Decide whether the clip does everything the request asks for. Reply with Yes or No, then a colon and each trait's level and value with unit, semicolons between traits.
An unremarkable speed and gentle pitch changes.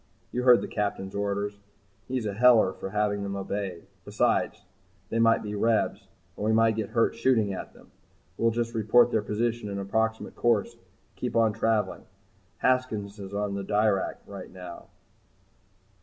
Yes: average, 165 wpm; narrow, 2.2 semitones